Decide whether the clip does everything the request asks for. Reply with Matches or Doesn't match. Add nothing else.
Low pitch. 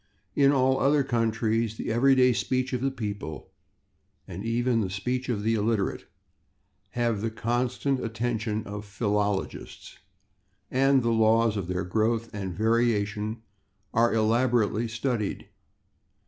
Matches